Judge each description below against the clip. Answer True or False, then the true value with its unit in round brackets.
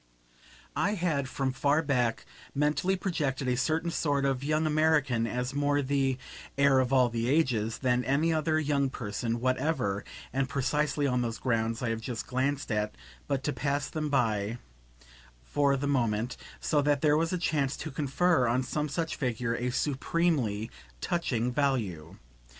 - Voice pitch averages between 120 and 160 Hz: True (135 Hz)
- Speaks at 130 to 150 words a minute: False (160 wpm)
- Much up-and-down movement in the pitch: False (3.5 semitones)